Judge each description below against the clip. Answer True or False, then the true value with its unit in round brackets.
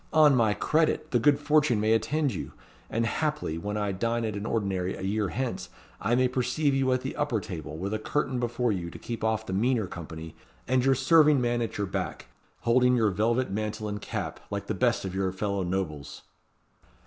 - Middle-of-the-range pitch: False (115 Hz)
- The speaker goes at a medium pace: False (210 wpm)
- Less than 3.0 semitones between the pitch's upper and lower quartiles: False (4.6 semitones)